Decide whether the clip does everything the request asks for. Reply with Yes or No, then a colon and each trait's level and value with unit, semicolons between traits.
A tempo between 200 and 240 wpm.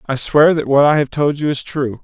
No: fast, 295 wpm